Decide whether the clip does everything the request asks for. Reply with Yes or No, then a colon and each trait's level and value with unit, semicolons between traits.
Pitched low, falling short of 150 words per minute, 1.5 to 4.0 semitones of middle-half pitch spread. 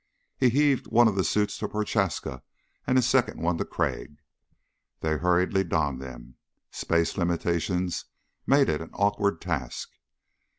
No: very low, 90 Hz; average, 140 wpm; average, 4.8 semitones